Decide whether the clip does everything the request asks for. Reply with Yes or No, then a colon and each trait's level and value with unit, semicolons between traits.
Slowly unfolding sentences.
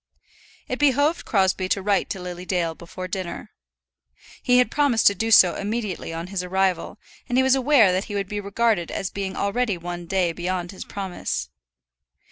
No: average, 180 wpm